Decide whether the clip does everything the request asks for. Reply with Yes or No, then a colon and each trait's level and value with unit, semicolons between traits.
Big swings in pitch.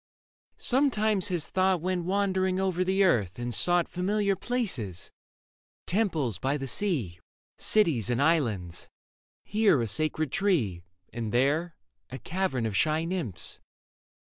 Yes: wide, 7.8 semitones